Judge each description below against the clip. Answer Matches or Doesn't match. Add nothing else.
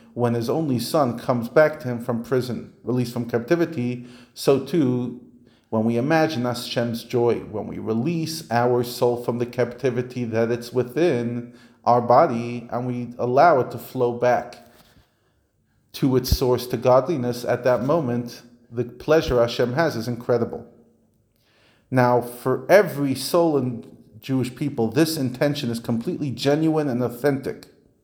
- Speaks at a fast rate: Doesn't match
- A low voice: Matches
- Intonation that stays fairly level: Matches